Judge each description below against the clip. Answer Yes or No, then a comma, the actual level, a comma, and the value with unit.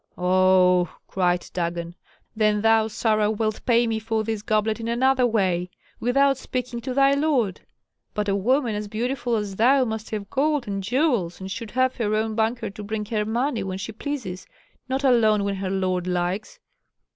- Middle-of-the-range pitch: No, high, 220 Hz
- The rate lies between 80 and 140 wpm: No, average, 180 wpm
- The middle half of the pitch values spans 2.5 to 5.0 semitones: Yes, average, 3.9 semitones